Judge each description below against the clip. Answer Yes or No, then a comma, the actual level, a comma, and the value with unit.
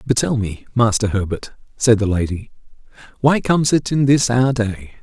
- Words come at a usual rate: Yes, average, 180 wpm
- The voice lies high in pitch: No, low, 115 Hz